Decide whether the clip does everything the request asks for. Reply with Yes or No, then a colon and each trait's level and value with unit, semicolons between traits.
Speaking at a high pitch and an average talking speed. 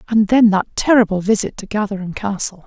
Yes: high, 205 Hz; average, 180 wpm